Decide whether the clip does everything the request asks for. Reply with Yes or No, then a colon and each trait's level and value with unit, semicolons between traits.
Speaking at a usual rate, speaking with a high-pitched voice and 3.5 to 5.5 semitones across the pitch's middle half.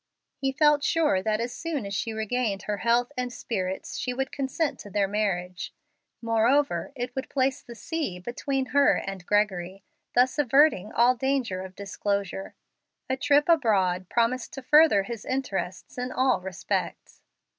Yes: average, 155 wpm; high, 235 Hz; average, 5.2 semitones